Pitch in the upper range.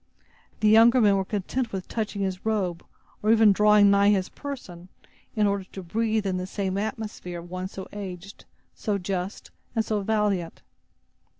Yes: high, 200 Hz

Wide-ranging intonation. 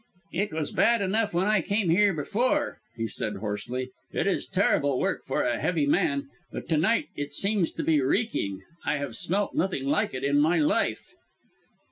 Yes: wide, 6.3 semitones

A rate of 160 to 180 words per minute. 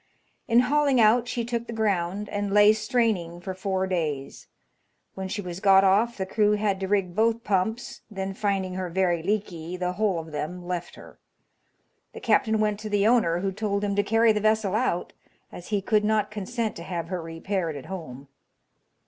No: average, 190 wpm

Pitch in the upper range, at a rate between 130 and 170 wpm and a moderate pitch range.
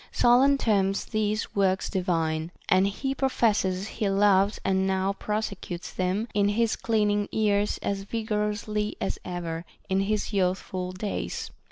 No: high, 200 Hz; average, 140 wpm; narrow, 2.2 semitones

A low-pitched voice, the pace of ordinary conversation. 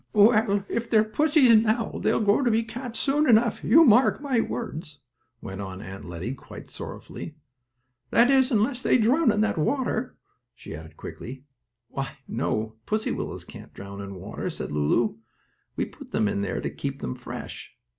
No: high, 215 Hz; average, 170 wpm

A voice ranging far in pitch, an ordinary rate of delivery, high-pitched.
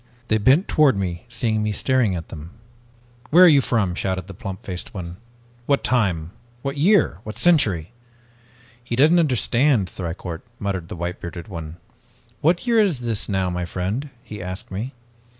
No: wide, 7.0 semitones; average, 170 wpm; low, 105 Hz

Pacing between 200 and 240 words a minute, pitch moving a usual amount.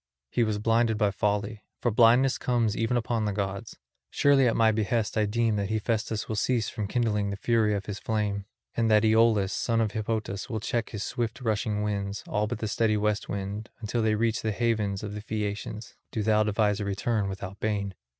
No: fast, 205 wpm; narrow, 1.7 semitones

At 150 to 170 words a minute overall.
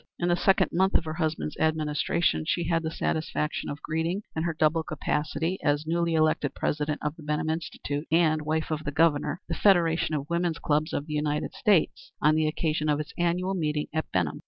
No: fast, 205 wpm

